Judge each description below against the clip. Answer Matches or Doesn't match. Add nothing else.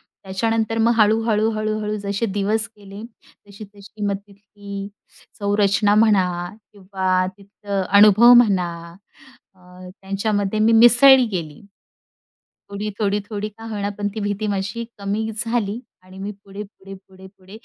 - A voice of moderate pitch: Doesn't match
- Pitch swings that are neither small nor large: Doesn't match